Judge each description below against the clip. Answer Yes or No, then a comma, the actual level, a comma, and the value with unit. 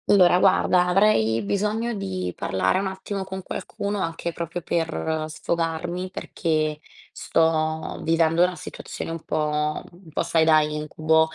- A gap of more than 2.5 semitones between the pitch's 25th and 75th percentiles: Yes, average, 2.9 semitones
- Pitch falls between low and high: Yes, medium, 165 Hz